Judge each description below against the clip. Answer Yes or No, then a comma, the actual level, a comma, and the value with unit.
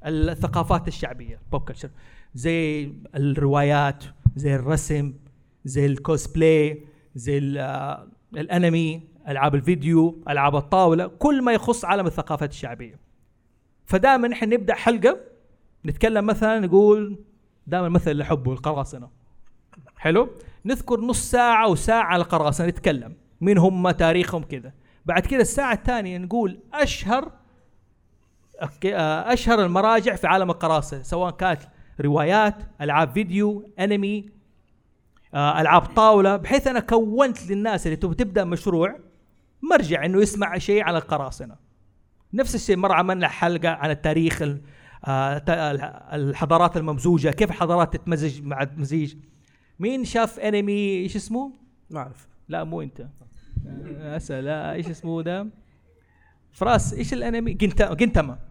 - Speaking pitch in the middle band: Yes, medium, 165 Hz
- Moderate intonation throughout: No, wide, 6.2 semitones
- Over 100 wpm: Yes, average, 110 wpm